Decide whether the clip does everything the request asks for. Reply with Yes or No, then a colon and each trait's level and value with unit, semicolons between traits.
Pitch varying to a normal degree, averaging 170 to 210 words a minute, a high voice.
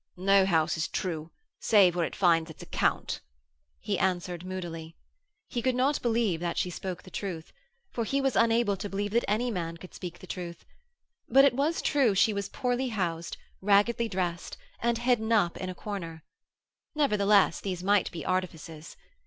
Yes: average, 4.9 semitones; average, 175 wpm; high, 195 Hz